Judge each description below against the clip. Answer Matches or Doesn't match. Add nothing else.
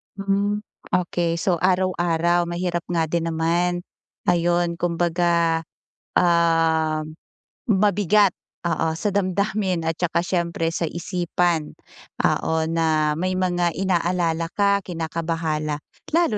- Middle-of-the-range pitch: Matches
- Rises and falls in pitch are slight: Matches